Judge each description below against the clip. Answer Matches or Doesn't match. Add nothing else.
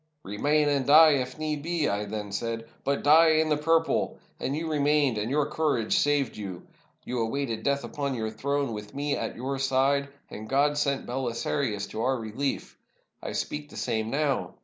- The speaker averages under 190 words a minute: Doesn't match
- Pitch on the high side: Doesn't match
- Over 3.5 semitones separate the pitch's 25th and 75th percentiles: Matches